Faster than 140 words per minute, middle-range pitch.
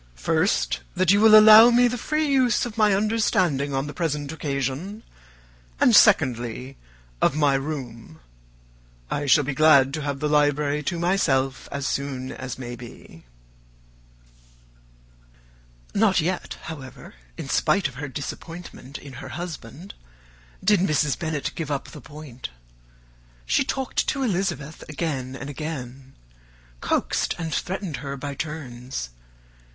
No: slow, 135 wpm; medium, 150 Hz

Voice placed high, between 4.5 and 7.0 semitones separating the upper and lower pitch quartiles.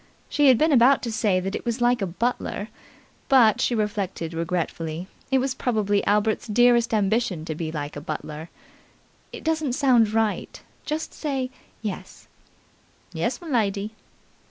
Yes: high, 220 Hz; average, 5.0 semitones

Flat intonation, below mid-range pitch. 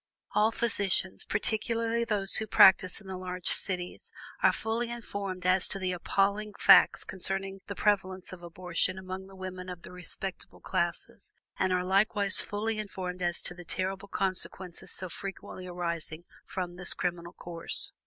No: narrow, 1.8 semitones; high, 190 Hz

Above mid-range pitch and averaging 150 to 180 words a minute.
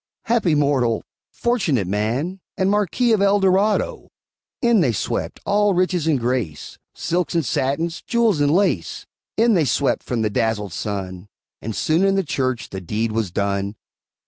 No: medium, 150 Hz; average, 160 wpm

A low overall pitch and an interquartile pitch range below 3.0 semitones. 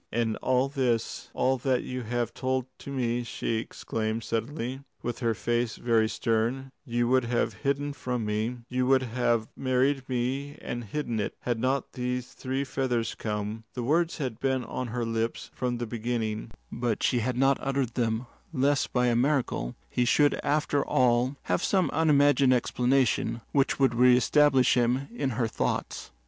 Yes: low, 125 Hz; narrow, 2.4 semitones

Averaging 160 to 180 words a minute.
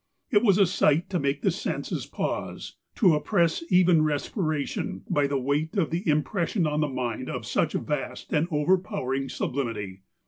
Yes: average, 170 wpm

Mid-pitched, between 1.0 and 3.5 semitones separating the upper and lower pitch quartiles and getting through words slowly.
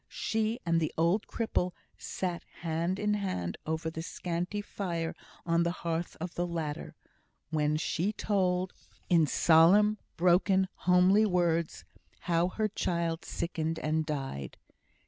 Yes: medium, 170 Hz; narrow, 2.6 semitones; slow, 130 wpm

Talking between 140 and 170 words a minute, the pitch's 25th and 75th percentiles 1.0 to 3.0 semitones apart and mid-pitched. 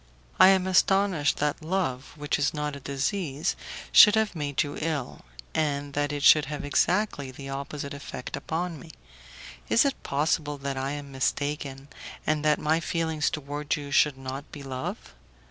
Yes: average, 165 wpm; narrow, 2.5 semitones; medium, 145 Hz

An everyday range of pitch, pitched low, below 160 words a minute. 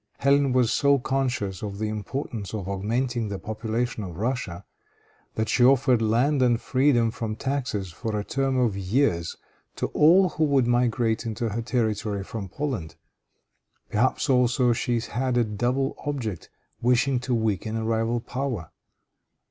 Yes: average, 3.4 semitones; low, 120 Hz; average, 150 wpm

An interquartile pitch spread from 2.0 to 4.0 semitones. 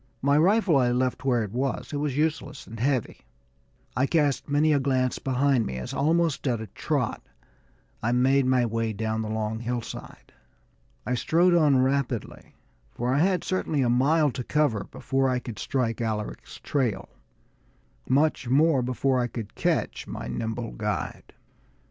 Yes: average, 3.6 semitones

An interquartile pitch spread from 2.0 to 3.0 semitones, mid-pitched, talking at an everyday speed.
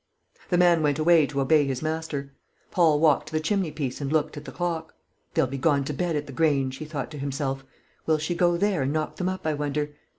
No: average, 2.7 semitones; medium, 155 Hz; fast, 235 wpm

